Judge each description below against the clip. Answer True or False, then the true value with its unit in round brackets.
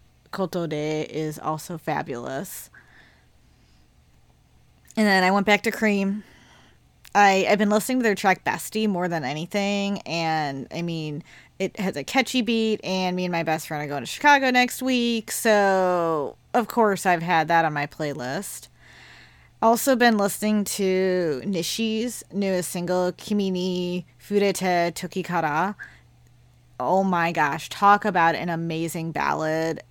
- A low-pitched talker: False (180 Hz)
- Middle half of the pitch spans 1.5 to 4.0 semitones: False (4.6 semitones)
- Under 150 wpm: True (140 wpm)